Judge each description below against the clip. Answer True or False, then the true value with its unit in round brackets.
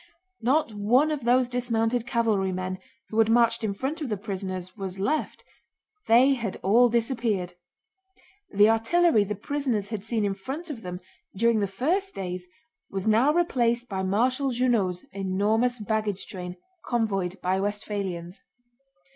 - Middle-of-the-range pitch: False (220 Hz)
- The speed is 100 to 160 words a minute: True (145 wpm)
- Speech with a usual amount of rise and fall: True (4.1 semitones)